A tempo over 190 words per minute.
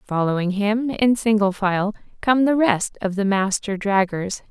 No: average, 160 wpm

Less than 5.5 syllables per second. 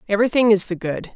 No: 7.2 syllables/s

